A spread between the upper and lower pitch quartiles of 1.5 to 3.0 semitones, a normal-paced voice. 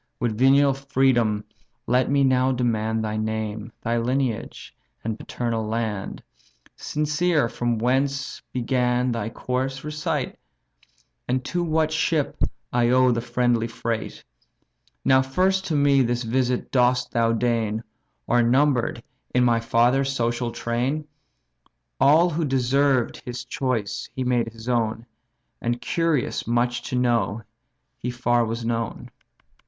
No: narrow, 2.6 semitones; slow, 130 wpm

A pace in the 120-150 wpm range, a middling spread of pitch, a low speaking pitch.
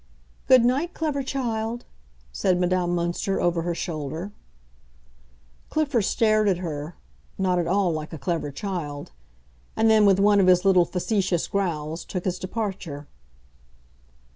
No: slow, 135 wpm; average, 4.2 semitones; medium, 185 Hz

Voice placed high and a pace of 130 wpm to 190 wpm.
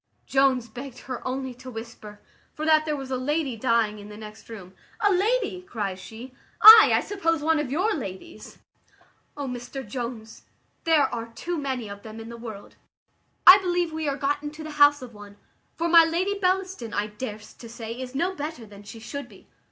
No: very high, 260 Hz; average, 200 wpm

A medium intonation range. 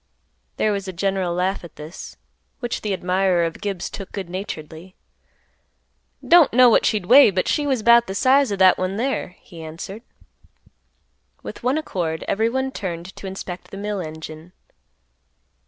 Yes: average, 4.2 semitones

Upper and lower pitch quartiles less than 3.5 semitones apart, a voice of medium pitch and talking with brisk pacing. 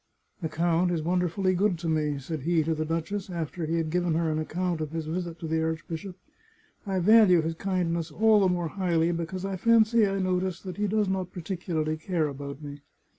Yes: average, 2.7 semitones; medium, 170 Hz; fast, 225 wpm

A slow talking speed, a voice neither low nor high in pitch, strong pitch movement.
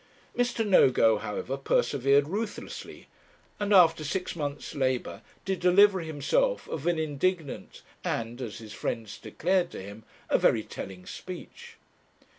Yes: slow, 130 wpm; medium, 160 Hz; wide, 6.7 semitones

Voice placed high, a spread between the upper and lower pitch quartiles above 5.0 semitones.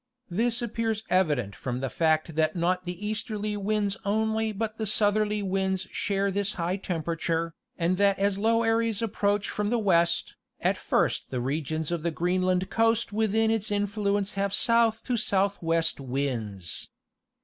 No: high, 200 Hz; average, 4.2 semitones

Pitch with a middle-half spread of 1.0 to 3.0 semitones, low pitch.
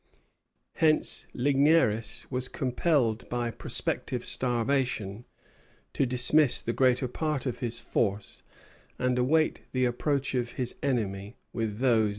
Yes: average, 2.7 semitones; low, 125 Hz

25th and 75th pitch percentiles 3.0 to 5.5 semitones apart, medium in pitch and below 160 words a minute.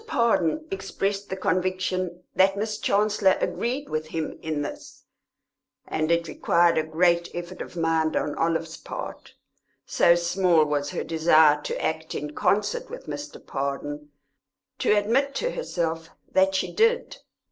Yes: average, 4.1 semitones; medium, 175 Hz; average, 145 wpm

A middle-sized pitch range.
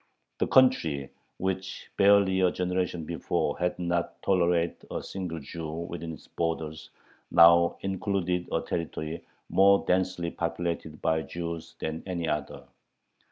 No: narrow, 2.2 semitones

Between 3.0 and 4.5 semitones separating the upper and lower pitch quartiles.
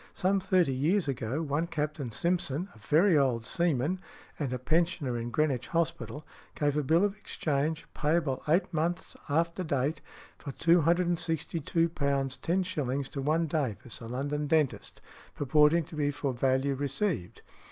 Yes: average, 3.7 semitones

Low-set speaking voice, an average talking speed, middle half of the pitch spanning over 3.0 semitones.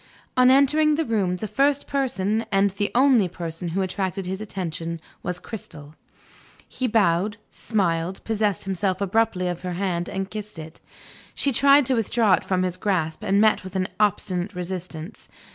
No: high, 195 Hz; average, 165 wpm; average, 3.8 semitones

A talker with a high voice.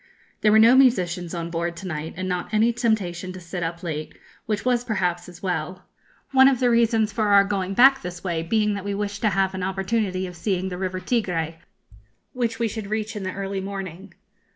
Yes: high, 195 Hz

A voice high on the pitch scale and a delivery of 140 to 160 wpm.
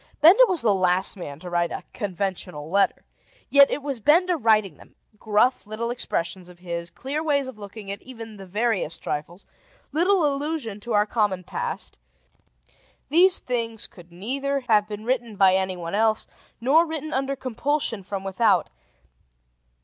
Yes: high, 220 Hz; average, 155 wpm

